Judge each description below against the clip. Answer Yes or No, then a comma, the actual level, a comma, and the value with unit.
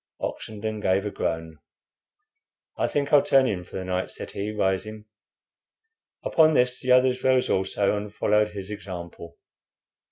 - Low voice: Yes, low, 105 Hz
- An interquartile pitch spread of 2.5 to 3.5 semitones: No, average, 5.0 semitones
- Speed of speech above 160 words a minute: No, average, 150 wpm